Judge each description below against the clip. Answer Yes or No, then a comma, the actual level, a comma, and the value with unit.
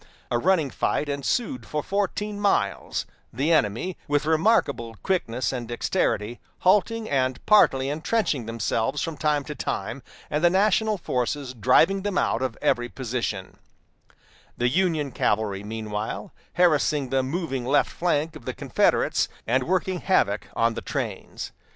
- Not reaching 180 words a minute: Yes, average, 140 wpm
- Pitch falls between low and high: Yes, medium, 145 Hz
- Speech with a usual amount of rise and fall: No, wide, 6.8 semitones